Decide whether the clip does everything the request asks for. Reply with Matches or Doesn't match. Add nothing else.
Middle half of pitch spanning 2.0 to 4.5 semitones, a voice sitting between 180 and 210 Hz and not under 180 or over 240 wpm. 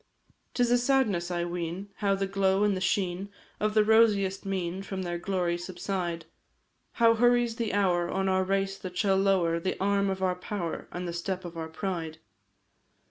Matches